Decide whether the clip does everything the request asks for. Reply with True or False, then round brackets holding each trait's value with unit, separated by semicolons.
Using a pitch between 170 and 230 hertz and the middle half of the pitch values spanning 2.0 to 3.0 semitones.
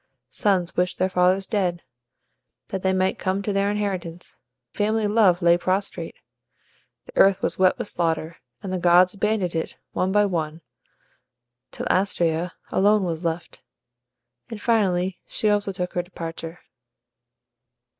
True (185 Hz; 2.5 semitones)